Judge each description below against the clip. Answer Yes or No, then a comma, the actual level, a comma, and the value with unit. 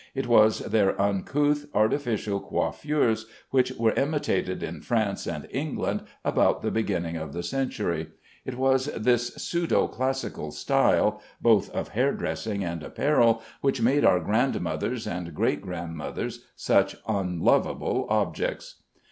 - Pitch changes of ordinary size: No, wide, 6.3 semitones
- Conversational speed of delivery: No, slow, 130 wpm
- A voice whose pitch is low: Yes, low, 110 Hz